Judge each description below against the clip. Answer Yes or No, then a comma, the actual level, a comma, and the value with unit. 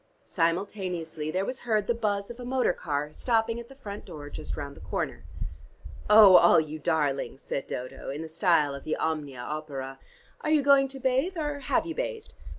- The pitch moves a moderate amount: No, wide, 8.7 semitones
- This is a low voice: No, medium, 185 Hz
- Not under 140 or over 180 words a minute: No, average, 195 wpm